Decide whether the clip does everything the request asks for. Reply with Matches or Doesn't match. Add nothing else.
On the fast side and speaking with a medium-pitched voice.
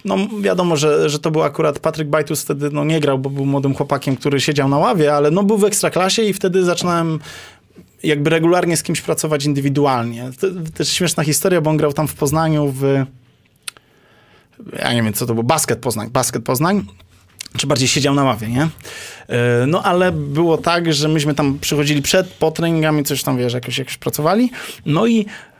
Matches